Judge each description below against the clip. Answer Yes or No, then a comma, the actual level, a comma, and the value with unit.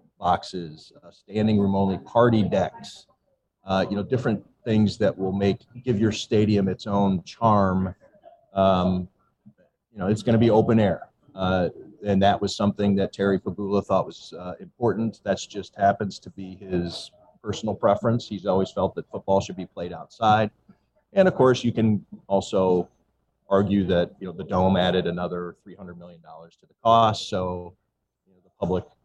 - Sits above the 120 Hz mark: No, low, 100 Hz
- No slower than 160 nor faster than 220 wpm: Yes, average, 175 wpm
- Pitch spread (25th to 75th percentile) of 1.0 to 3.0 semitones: Yes, narrow, 2.6 semitones